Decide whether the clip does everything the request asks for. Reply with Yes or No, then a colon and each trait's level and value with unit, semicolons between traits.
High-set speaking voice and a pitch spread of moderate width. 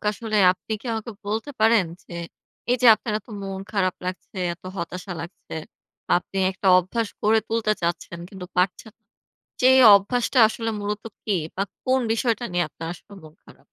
Yes: high, 205 Hz; average, 3.6 semitones